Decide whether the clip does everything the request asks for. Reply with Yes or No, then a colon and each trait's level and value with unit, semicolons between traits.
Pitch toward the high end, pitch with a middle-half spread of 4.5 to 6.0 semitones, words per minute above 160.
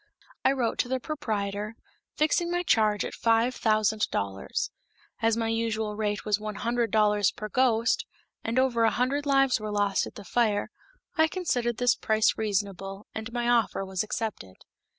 No: high, 220 Hz; average, 2.7 semitones; average, 170 wpm